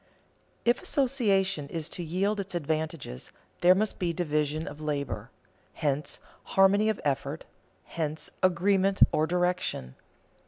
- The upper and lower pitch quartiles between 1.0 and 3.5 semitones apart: No, average, 4.1 semitones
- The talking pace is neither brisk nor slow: No, slow, 120 wpm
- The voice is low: No, medium, 175 Hz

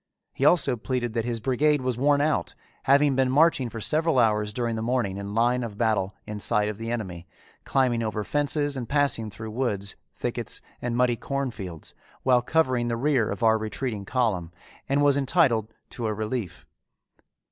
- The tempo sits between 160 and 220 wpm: Yes, average, 180 wpm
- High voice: No, low, 120 Hz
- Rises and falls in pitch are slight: No, average, 3.8 semitones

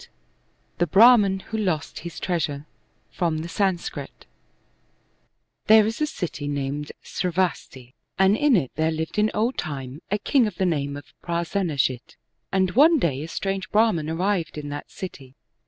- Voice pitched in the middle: Yes, medium, 175 Hz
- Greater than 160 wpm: No, average, 155 wpm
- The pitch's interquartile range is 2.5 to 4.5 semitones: No, average, 5.3 semitones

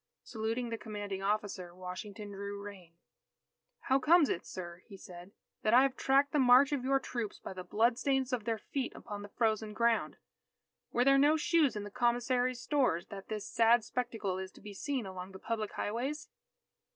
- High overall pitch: Yes, high, 225 Hz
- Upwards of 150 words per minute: Yes, average, 185 wpm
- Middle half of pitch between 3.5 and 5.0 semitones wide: Yes, average, 4.1 semitones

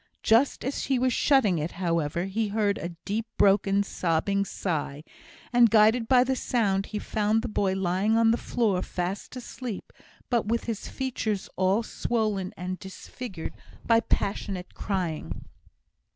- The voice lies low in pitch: No, high, 205 Hz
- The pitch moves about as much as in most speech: Yes, average, 3.6 semitones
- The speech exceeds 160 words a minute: No, average, 150 wpm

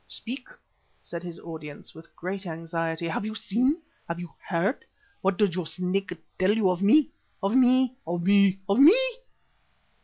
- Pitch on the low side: No, high, 190 Hz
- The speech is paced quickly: No, average, 160 wpm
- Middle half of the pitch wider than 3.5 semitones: Yes, average, 4.3 semitones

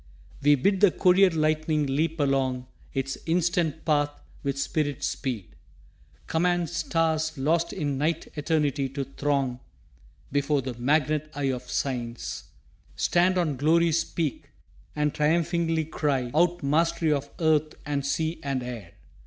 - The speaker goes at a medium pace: No, slow, 130 wpm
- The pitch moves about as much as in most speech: Yes, average, 3.1 semitones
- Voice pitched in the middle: Yes, medium, 150 Hz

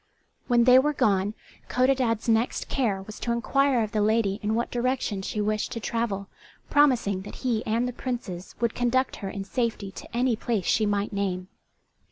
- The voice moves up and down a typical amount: Yes, average, 3.3 semitones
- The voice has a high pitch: Yes, high, 225 Hz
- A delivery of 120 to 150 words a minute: No, average, 185 wpm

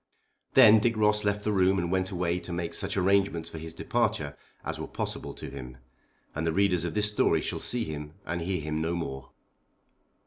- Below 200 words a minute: No, fast, 205 wpm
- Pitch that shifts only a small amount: No, average, 4.2 semitones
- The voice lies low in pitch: Yes, very low, 90 Hz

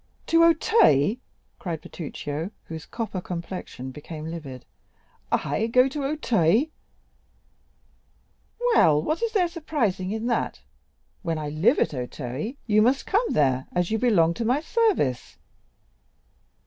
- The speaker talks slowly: Yes, slow, 120 wpm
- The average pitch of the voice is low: No, high, 195 Hz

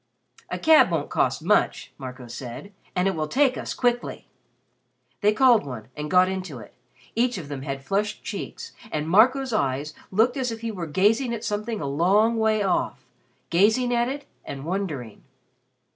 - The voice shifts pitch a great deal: Yes, wide, 7.8 semitones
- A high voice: Yes, high, 200 Hz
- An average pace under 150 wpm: No, average, 175 wpm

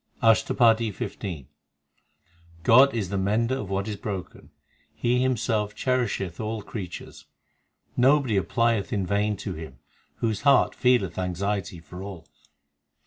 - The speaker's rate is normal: No, slow, 130 wpm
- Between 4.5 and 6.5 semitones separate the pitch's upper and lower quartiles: No, average, 3.5 semitones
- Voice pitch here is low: Yes, low, 105 Hz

